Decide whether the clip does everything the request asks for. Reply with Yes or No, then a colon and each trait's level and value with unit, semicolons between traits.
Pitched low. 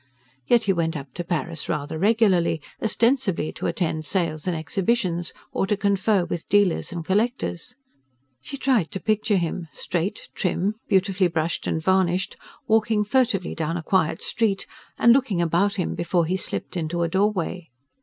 No: medium, 185 Hz